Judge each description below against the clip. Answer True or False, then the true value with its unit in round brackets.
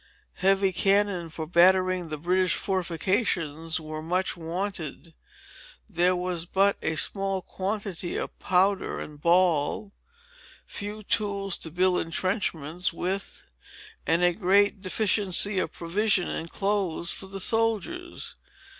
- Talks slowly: True (120 wpm)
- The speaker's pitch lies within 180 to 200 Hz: True (185 Hz)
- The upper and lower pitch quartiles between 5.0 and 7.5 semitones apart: False (2.8 semitones)